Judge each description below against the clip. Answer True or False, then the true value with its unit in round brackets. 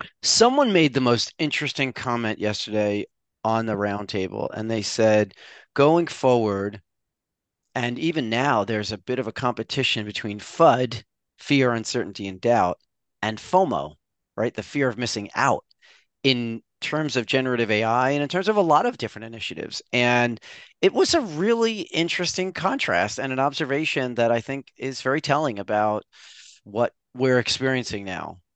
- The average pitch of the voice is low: True (120 Hz)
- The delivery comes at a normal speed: True (155 wpm)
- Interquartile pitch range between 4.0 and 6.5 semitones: True (4.7 semitones)